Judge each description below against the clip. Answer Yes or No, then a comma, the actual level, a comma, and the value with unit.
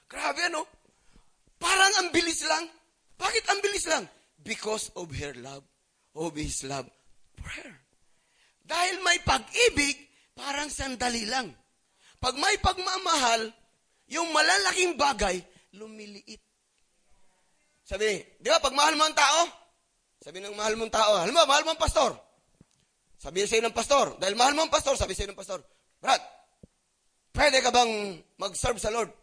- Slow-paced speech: No, average, 145 wpm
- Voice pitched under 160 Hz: No, very high, 265 Hz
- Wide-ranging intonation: Yes, wide, 7.6 semitones